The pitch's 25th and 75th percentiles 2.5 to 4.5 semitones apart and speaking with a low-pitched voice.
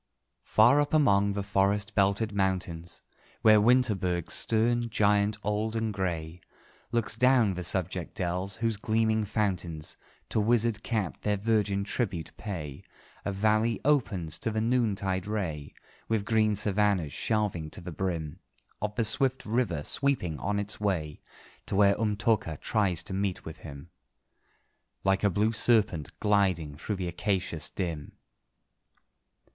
Yes: average, 3.4 semitones; low, 100 Hz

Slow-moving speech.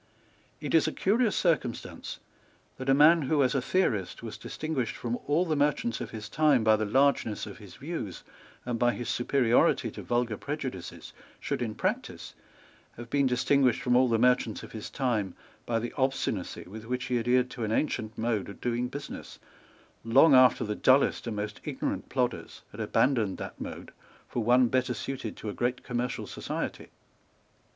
No: average, 175 wpm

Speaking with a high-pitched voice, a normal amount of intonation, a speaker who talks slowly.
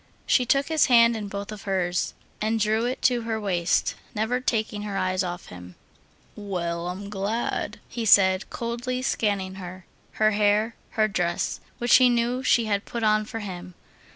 No: high, 210 Hz; average, 3.7 semitones; average, 175 wpm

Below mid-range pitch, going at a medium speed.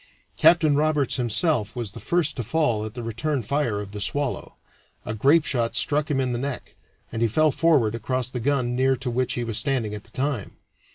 No: low, 130 Hz; fast, 210 wpm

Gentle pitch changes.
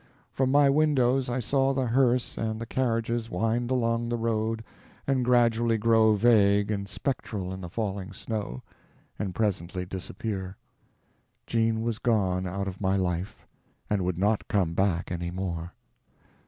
No: average, 3.9 semitones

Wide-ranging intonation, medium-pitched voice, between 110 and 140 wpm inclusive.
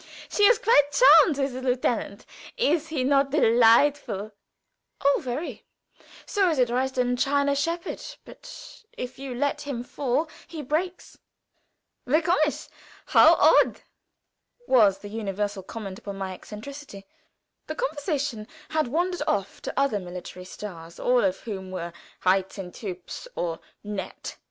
No: wide, 6.3 semitones; very high, 250 Hz; slow, 135 wpm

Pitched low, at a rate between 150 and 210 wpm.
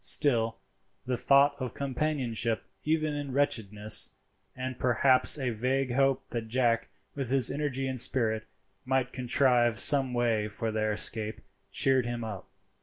No: low, 125 Hz; average, 140 wpm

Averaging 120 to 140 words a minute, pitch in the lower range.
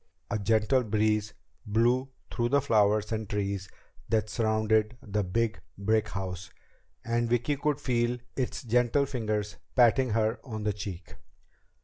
Yes: slow, 135 wpm; low, 110 Hz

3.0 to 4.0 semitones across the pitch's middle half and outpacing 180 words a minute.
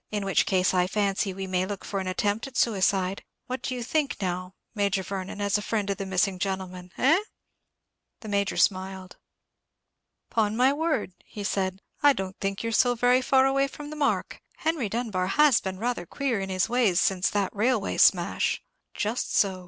No: average, 4.5 semitones; average, 190 wpm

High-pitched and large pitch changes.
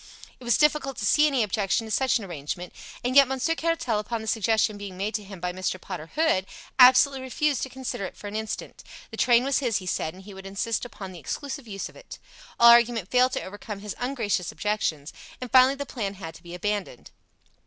No: high, 220 Hz; average, 4.8 semitones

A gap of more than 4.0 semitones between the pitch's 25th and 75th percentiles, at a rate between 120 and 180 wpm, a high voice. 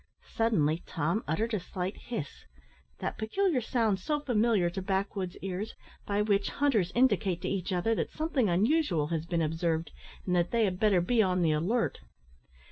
Yes: average, 4.6 semitones; average, 170 wpm; high, 195 Hz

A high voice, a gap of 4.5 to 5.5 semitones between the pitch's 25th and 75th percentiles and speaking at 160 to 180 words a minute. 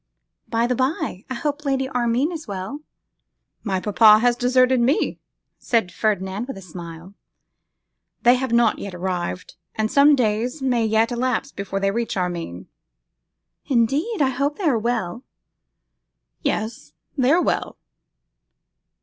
No: high, 235 Hz; average, 5.0 semitones; average, 140 wpm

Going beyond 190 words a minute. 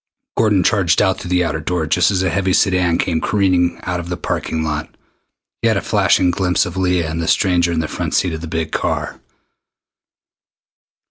Yes: average, 200 wpm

